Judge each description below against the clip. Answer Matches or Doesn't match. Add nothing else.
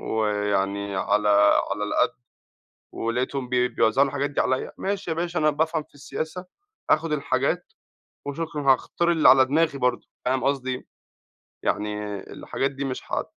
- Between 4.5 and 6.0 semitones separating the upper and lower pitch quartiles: Matches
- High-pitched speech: Doesn't match